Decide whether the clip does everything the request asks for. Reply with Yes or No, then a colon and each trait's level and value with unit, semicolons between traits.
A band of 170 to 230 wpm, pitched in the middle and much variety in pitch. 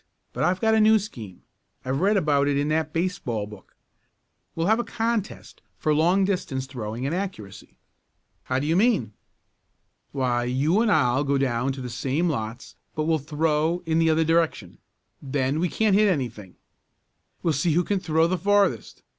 Yes: average, 180 wpm; medium, 155 Hz; wide, 5.7 semitones